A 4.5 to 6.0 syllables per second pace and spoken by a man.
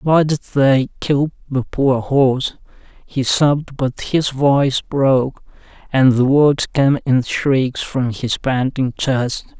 No: 3.5 syllables/s; male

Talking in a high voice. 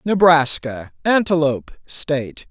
No: medium, 155 Hz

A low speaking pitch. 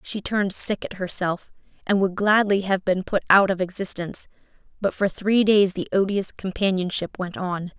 No: high, 190 Hz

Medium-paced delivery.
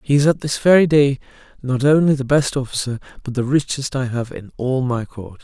No: fast, 220 wpm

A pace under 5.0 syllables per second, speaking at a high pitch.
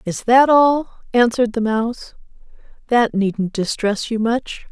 Yes: 4.1 syllables/s; high, 230 Hz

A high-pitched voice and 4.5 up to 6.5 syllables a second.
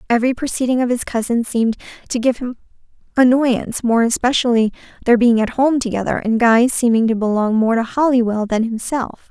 Yes: high, 235 Hz; 5.7 syllables/s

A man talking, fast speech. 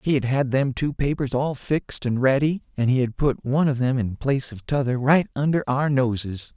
Yes: male; fast, 230 wpm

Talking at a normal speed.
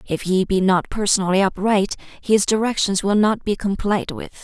Yes: average, 175 wpm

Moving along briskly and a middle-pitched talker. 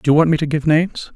Yes: fast, 365 wpm; medium, 155 Hz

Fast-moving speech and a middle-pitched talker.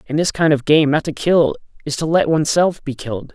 Yes: fast, 270 wpm; medium, 150 Hz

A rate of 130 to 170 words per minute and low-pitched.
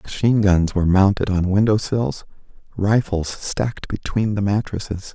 Yes: average, 140 wpm; low, 100 Hz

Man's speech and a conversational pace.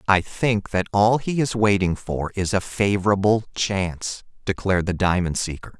Yes: male; average, 165 wpm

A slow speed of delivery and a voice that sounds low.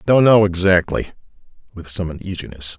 Yes: slow, 130 wpm; very low, 90 Hz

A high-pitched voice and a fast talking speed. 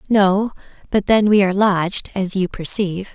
No: high, 195 Hz; average, 170 wpm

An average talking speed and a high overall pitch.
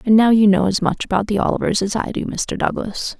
No: fast, 265 wpm; high, 210 Hz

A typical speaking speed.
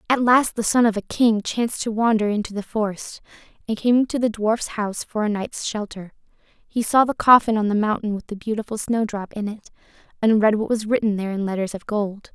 No: fast, 225 wpm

